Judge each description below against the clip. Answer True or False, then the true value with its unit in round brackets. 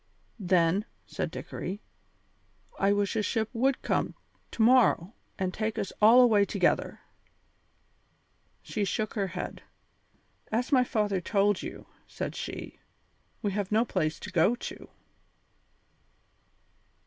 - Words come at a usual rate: False (125 wpm)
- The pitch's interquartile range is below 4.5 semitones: True (2.7 semitones)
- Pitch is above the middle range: True (205 Hz)